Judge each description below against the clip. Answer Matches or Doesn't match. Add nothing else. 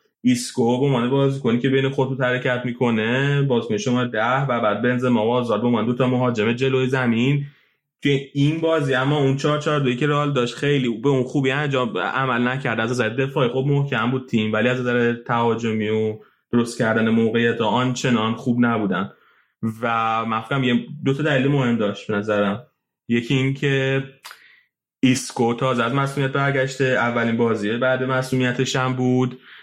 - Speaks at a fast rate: Matches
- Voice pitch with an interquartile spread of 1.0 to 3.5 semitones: Matches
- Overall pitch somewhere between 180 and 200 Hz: Doesn't match